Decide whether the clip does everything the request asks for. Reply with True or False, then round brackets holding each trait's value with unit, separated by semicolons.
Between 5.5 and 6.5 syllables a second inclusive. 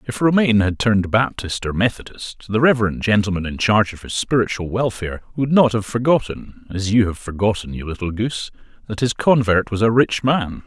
True (5.7 syllables/s)